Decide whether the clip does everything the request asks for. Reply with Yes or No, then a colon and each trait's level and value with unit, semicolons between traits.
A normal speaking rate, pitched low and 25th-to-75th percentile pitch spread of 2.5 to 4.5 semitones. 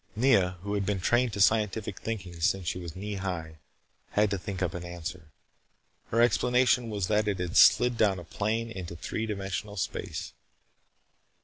Yes: average, 175 wpm; low, 100 Hz; average, 3.5 semitones